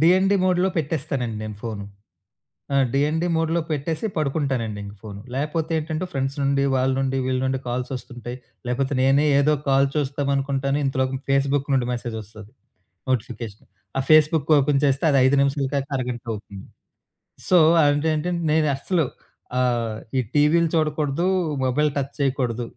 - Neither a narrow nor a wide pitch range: Yes, average, 3.2 semitones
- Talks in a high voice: No, medium, 140 Hz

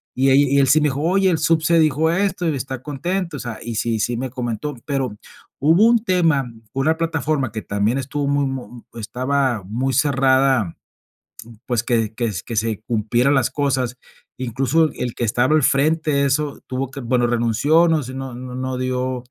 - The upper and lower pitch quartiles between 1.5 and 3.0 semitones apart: No, average, 3.7 semitones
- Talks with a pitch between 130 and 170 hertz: Yes, low, 135 Hz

